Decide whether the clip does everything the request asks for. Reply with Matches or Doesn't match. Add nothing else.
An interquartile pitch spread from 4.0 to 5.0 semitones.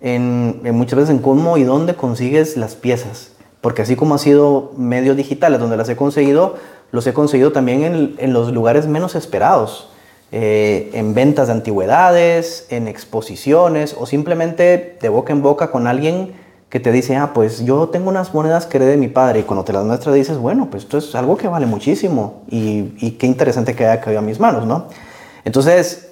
Matches